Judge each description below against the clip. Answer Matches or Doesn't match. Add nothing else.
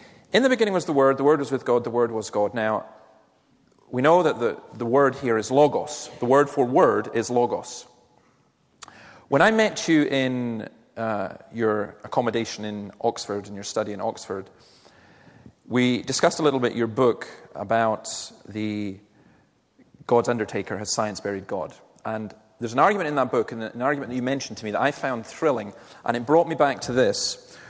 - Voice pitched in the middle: Doesn't match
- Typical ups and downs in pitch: Matches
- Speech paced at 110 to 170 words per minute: Doesn't match